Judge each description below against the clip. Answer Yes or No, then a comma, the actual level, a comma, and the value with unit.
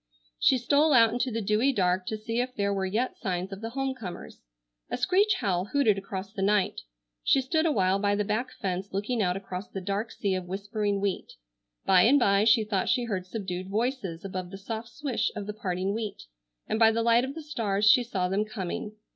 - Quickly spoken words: Yes, fast, 220 wpm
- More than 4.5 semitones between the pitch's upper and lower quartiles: No, average, 3.6 semitones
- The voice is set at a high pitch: Yes, high, 210 Hz